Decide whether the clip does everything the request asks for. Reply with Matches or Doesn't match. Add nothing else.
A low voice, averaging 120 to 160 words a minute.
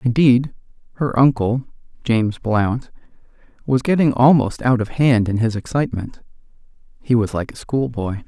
Matches